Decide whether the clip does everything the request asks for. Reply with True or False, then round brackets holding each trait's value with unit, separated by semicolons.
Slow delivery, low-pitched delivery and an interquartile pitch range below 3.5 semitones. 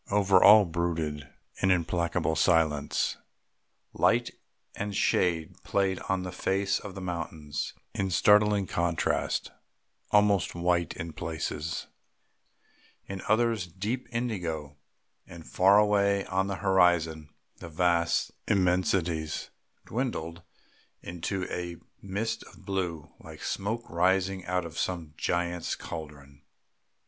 True (110 wpm; 90 Hz; 3.0 semitones)